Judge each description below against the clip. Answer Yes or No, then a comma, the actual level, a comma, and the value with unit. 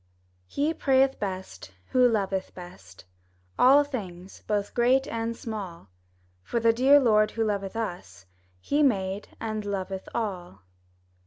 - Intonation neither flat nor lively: Yes, average, 4.4 semitones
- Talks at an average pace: No, slow, 130 wpm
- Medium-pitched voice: No, high, 210 Hz